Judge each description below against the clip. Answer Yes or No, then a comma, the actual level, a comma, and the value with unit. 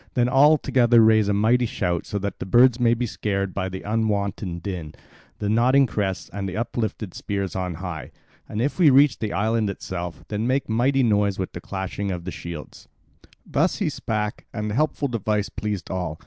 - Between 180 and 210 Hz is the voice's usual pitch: No, low, 105 Hz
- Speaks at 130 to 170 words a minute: No, average, 190 wpm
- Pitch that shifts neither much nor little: Yes, average, 4.0 semitones